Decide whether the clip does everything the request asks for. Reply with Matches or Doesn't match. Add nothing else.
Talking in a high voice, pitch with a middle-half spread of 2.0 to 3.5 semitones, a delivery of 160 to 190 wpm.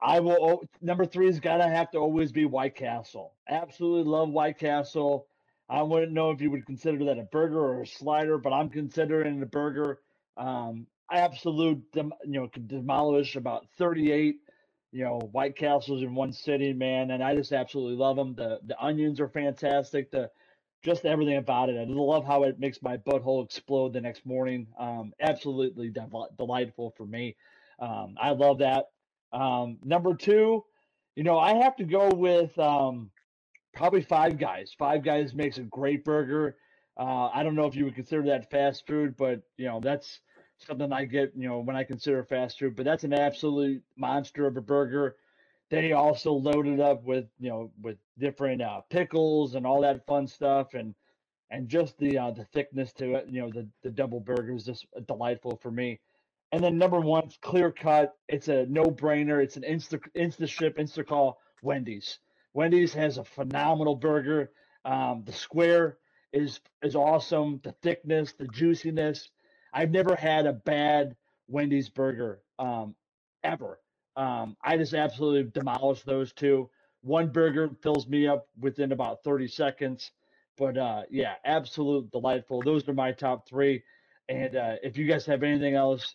Doesn't match